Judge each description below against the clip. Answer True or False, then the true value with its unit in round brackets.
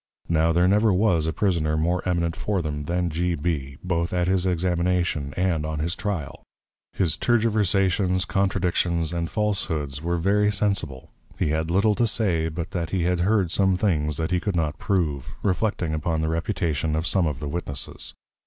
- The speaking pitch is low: True (85 Hz)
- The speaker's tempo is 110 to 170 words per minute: False (180 wpm)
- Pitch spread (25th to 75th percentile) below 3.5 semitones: True (3.1 semitones)